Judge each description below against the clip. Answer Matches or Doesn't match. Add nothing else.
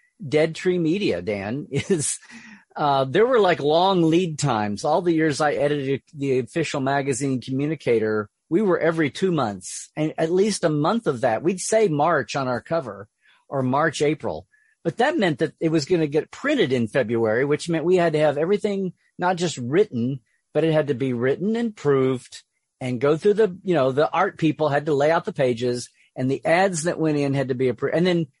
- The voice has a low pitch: Doesn't match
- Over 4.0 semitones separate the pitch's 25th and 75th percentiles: Matches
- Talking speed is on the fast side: Matches